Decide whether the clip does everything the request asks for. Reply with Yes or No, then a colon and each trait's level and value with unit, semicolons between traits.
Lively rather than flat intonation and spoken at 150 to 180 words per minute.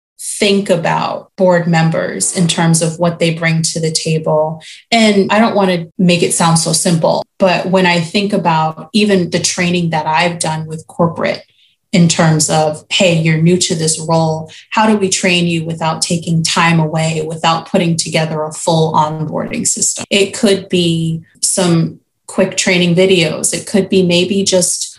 No: average, 2.8 semitones; average, 175 wpm